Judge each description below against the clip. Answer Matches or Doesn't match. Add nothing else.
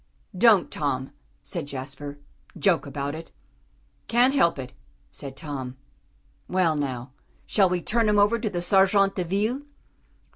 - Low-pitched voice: Doesn't match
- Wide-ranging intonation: Matches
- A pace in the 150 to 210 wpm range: Doesn't match